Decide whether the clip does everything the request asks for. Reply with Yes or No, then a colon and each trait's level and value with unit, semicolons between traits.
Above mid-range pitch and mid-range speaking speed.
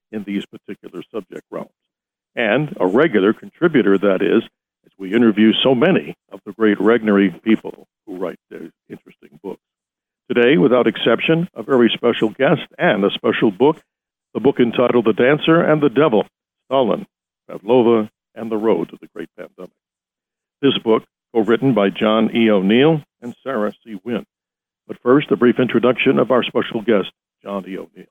No: low, 115 Hz; average, 165 wpm